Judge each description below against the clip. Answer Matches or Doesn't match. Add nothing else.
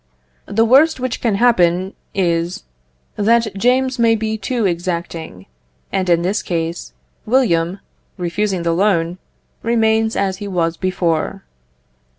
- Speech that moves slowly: Matches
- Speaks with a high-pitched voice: Matches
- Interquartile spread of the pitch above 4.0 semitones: Matches